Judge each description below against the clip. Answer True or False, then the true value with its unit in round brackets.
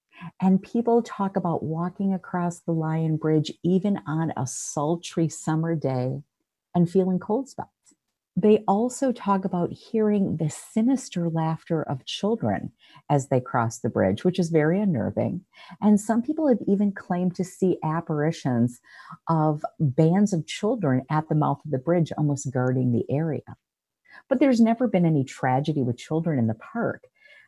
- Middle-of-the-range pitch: True (170 Hz)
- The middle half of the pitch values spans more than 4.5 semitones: True (4.9 semitones)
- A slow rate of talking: False (155 wpm)